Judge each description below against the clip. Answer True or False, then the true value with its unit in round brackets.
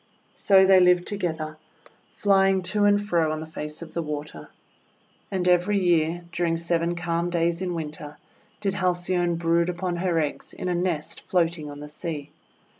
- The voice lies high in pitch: False (175 Hz)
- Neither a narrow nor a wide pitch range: False (2.3 semitones)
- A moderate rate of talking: True (170 wpm)